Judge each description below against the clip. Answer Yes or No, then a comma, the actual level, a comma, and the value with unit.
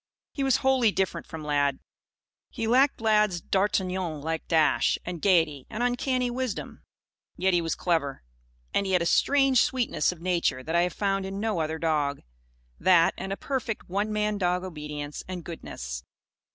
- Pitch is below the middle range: No, medium, 185 Hz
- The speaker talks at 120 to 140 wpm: No, average, 170 wpm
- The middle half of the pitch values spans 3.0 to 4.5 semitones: No, average, 4.9 semitones